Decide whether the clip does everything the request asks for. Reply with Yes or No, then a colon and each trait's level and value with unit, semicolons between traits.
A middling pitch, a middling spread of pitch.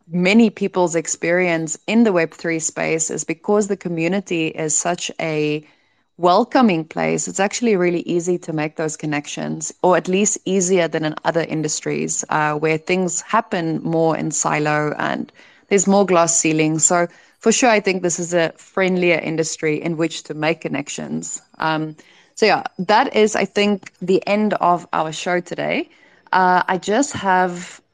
Yes: medium, 175 Hz; average, 3.4 semitones